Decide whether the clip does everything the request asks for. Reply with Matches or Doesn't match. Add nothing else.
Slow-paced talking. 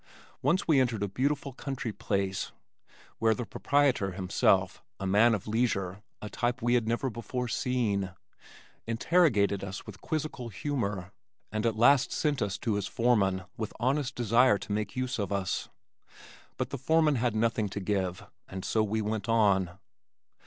Doesn't match